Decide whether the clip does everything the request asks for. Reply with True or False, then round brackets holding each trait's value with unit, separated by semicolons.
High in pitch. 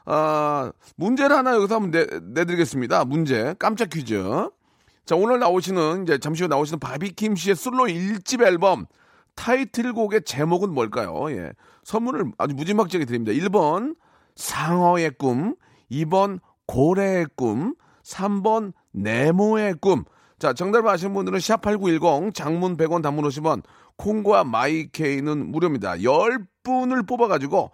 False (180 Hz)